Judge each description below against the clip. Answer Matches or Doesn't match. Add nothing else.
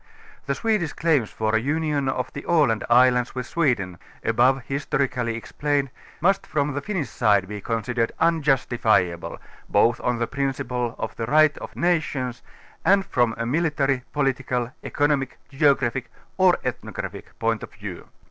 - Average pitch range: Matches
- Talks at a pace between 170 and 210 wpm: Doesn't match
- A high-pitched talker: Doesn't match